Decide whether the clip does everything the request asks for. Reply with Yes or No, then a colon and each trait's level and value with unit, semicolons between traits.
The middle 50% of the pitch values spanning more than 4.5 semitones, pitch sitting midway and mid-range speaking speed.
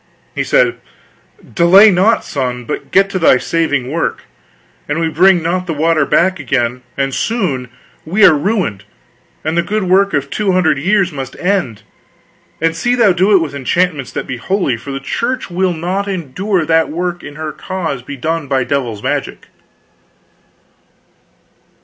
Yes: average, 5.2 semitones; medium, 165 Hz; average, 165 wpm